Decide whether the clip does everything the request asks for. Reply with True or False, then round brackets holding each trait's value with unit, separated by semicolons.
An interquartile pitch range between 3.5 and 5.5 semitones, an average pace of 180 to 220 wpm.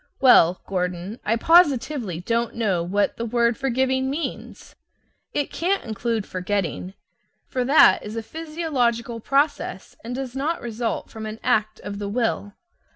False (4.5 semitones; 145 wpm)